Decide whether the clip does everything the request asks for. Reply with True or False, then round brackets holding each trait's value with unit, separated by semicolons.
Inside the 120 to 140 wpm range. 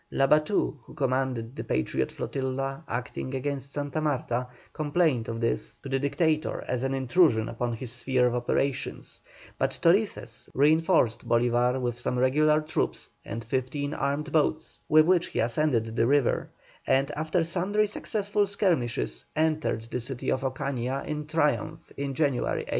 False (150 wpm)